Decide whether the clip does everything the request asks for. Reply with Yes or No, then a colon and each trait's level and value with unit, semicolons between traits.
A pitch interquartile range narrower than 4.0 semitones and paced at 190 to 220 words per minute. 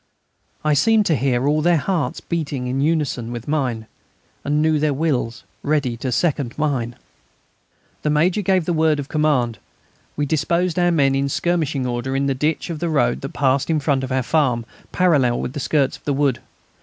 Yes: average, 3.4 semitones; average, 195 wpm